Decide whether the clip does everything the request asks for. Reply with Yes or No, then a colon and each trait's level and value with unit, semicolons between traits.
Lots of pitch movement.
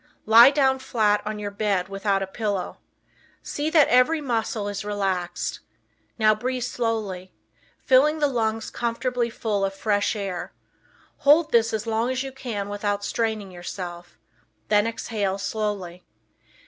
No: average, 3.4 semitones